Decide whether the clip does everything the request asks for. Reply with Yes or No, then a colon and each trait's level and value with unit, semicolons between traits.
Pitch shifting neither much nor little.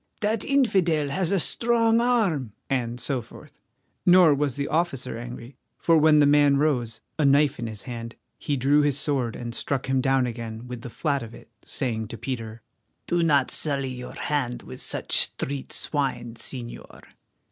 Yes: average, 4.1 semitones